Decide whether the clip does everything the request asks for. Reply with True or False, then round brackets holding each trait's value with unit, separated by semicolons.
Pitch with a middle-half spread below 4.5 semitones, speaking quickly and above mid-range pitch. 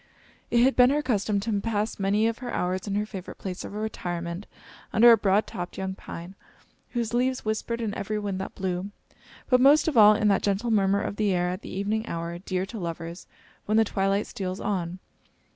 True (2.9 semitones; 210 wpm; 205 Hz)